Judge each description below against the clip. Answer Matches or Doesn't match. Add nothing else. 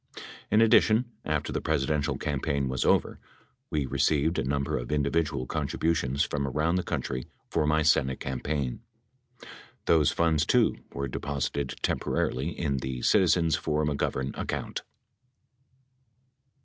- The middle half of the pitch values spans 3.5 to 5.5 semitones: Doesn't match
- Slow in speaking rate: Matches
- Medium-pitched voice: Doesn't match